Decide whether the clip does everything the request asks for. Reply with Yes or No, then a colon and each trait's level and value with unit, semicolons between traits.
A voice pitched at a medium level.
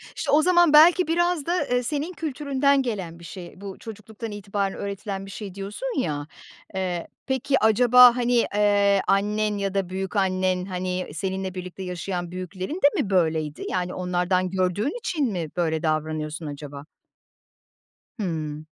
No: high, 195 Hz